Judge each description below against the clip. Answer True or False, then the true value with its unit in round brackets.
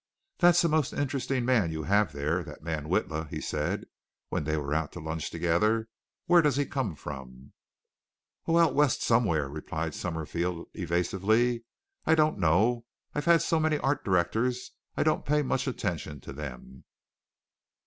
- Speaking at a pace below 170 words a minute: True (160 wpm)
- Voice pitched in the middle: False (95 Hz)